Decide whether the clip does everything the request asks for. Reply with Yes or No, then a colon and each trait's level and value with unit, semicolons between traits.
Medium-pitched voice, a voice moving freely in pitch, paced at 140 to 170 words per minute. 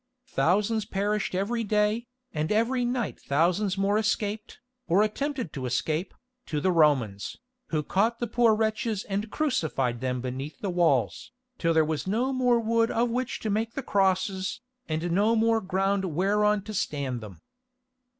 No: high, 200 Hz; wide, 5.7 semitones; average, 160 wpm